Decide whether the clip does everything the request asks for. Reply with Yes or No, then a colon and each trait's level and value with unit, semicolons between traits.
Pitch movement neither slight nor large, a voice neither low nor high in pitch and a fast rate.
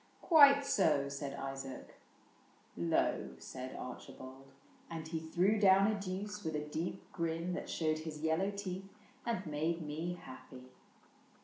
No: average, 4.7 semitones; medium, 160 Hz; average, 155 wpm